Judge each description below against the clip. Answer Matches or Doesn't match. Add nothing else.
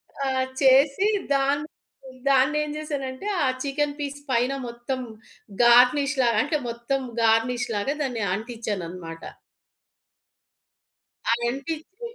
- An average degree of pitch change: Matches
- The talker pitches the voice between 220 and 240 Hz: Doesn't match